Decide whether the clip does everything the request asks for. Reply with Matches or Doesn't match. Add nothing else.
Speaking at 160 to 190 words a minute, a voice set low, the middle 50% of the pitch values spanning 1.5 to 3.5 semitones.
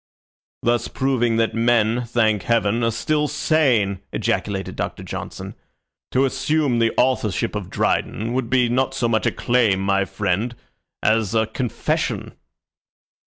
Doesn't match